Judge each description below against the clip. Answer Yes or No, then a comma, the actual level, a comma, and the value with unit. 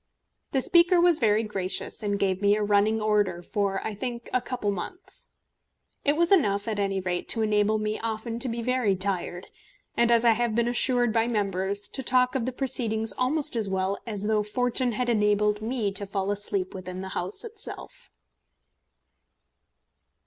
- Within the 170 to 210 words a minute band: Yes, average, 180 wpm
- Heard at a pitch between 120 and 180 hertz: No, high, 215 Hz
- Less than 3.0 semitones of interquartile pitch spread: No, average, 3.3 semitones